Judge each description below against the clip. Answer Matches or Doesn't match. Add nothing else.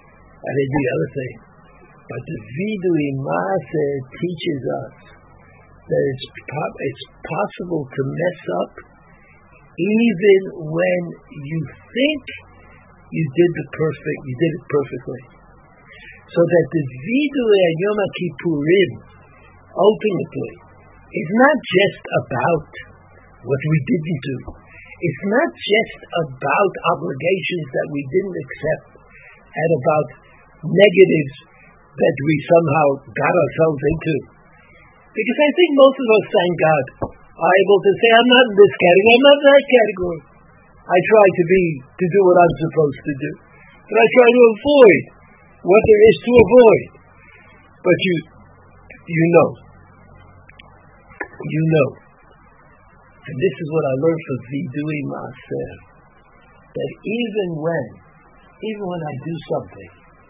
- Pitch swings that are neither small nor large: Doesn't match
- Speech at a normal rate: Doesn't match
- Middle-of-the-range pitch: Matches